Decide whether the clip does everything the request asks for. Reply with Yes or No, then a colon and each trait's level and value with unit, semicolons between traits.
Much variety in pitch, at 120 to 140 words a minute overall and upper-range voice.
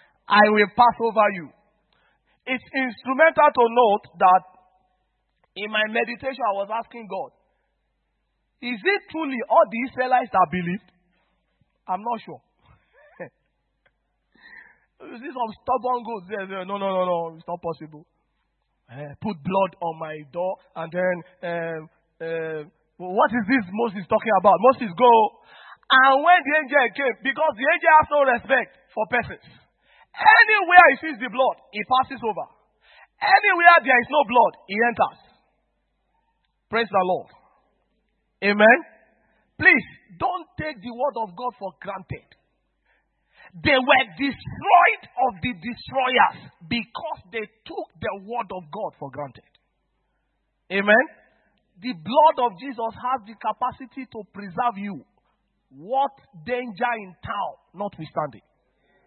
Yes: wide, 5.8 semitones; slow, 135 wpm; high, 230 Hz